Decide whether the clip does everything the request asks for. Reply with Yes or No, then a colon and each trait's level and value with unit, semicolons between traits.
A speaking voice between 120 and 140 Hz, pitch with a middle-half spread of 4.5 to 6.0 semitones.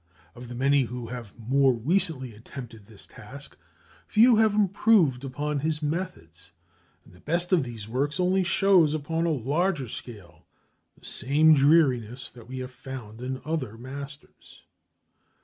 Yes: low, 135 Hz; average, 5.1 semitones